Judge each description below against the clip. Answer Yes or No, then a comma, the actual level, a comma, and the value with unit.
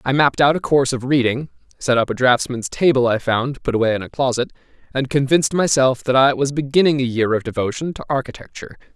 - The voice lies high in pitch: No, low, 130 Hz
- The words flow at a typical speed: No, fast, 215 wpm